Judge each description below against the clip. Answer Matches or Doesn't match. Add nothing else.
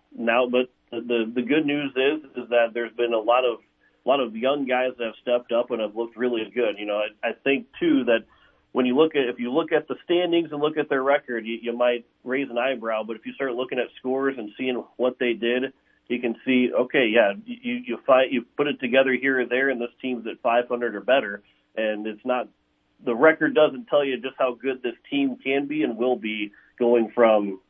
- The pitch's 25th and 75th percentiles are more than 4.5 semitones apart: Doesn't match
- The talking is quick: Matches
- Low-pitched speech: Matches